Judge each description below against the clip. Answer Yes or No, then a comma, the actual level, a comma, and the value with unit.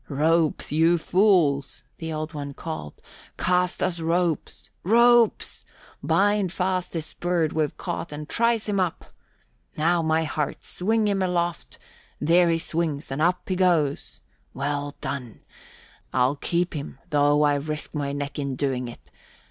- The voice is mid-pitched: Yes, medium, 160 Hz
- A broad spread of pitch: No, average, 3.7 semitones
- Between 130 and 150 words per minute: Yes, average, 145 wpm